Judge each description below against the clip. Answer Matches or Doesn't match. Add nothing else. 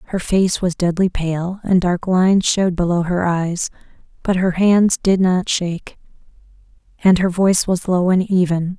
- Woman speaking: Matches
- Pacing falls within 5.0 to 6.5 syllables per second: Doesn't match